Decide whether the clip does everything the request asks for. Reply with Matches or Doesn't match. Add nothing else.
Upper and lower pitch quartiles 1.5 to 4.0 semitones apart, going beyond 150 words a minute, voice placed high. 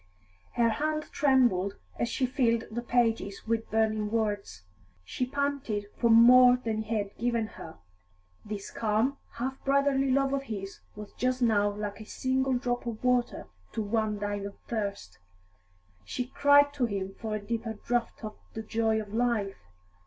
Matches